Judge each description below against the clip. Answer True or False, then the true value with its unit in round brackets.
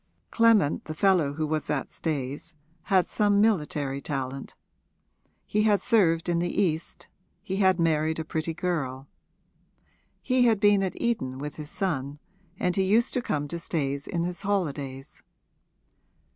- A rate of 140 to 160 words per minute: True (150 wpm)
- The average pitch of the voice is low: False (165 Hz)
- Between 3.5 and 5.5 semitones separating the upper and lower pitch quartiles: True (5.2 semitones)